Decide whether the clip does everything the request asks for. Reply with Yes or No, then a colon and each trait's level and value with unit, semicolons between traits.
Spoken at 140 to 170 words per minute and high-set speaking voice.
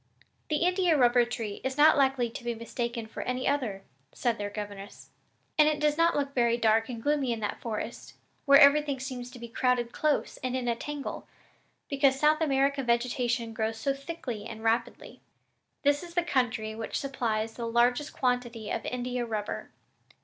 No: average, 180 wpm; high, 245 Hz